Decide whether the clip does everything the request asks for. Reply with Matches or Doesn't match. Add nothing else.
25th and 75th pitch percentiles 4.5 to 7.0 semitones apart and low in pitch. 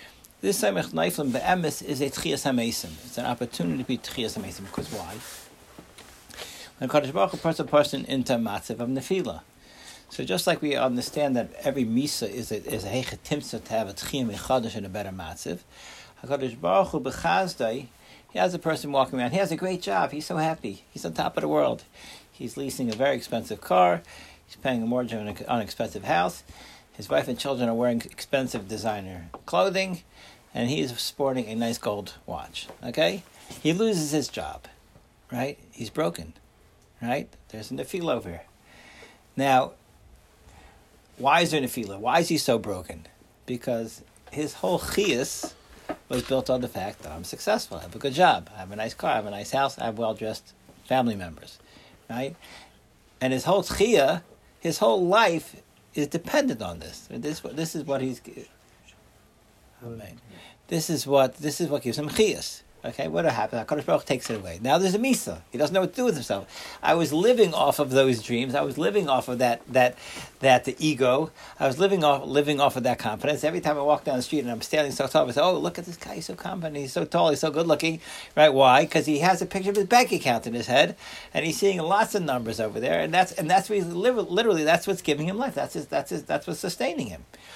Matches